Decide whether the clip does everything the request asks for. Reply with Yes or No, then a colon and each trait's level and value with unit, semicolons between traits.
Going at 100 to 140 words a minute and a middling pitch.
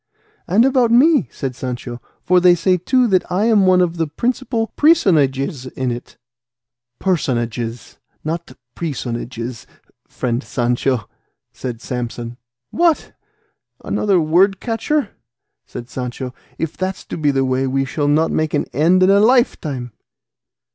Yes: slow, 135 wpm; medium, 155 Hz